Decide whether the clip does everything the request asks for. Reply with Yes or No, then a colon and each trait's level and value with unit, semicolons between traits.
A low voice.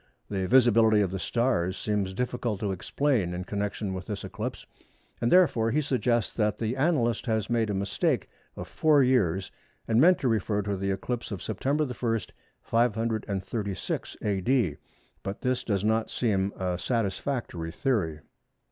Yes: low, 110 Hz